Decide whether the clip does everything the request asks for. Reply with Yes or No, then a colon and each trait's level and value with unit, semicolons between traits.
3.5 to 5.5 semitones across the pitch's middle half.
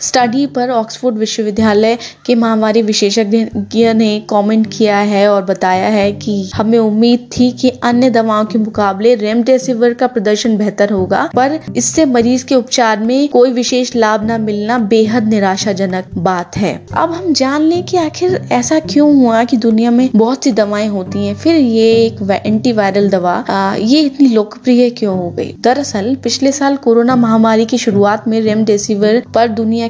No: average, 2.8 semitones